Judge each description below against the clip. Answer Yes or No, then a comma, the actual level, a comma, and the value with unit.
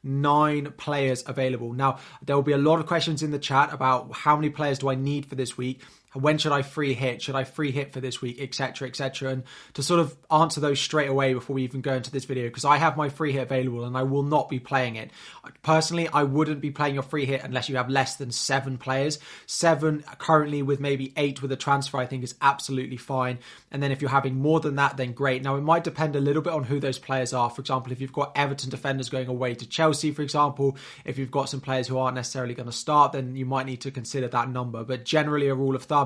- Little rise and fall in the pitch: Yes, narrow, 2.1 semitones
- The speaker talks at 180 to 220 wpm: No, fast, 260 wpm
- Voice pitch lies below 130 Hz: No, low, 135 Hz